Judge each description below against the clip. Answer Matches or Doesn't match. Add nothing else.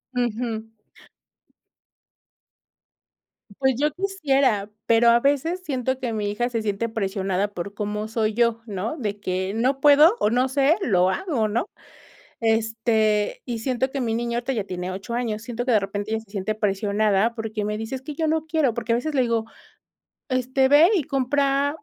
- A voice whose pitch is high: Matches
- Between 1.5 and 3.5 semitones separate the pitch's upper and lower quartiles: Doesn't match